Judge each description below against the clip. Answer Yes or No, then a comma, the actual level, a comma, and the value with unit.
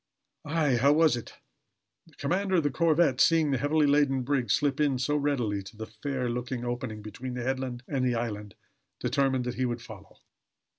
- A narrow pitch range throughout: No, average, 3.3 semitones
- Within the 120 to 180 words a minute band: No, average, 190 wpm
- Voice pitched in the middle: No, low, 130 Hz